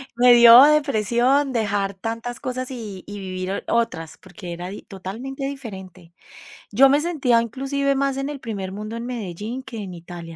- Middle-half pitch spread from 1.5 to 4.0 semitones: No, wide, 5.5 semitones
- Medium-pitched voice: No, high, 230 Hz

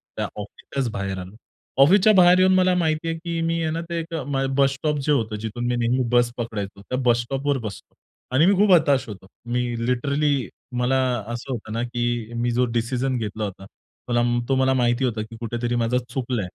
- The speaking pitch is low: Yes, low, 125 Hz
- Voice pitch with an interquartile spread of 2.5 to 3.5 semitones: No, average, 4.2 semitones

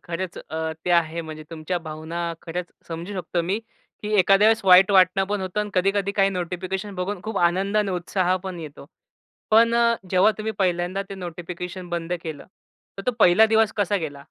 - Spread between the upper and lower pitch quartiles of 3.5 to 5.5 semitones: No, narrow, 2.6 semitones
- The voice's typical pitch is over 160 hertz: Yes, medium, 185 Hz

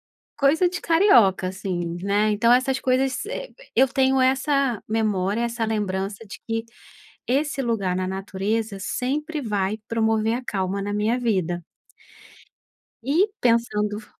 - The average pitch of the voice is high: Yes, high, 225 Hz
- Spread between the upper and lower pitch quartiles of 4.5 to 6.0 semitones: Yes, average, 4.8 semitones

